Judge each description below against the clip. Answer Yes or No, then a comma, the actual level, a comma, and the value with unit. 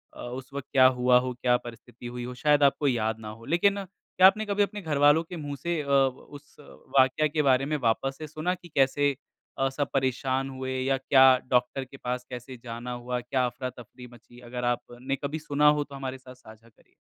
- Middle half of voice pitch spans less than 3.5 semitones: Yes, average, 2.8 semitones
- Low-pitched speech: Yes, low, 130 Hz